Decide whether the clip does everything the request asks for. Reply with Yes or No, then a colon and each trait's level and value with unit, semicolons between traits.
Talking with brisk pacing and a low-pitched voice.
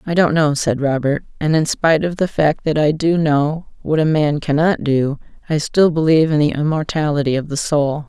No: fast, 215 wpm; medium, 150 Hz